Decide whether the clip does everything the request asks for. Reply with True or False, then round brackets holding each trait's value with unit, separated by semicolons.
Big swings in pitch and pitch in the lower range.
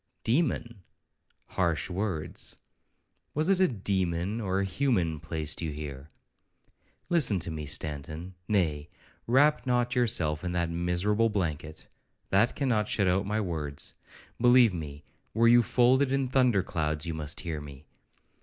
True (7.0 semitones; 95 Hz)